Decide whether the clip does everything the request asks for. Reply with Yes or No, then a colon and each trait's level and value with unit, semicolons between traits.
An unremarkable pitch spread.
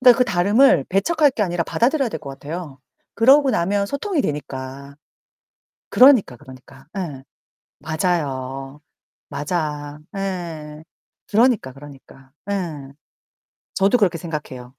No: wide, 6.7 semitones